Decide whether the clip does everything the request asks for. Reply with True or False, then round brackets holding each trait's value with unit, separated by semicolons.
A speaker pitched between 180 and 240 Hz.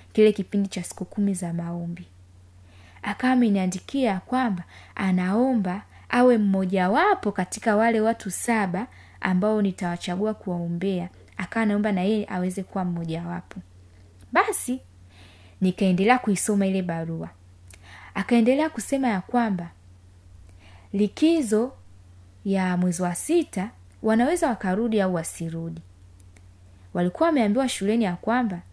True (185 Hz)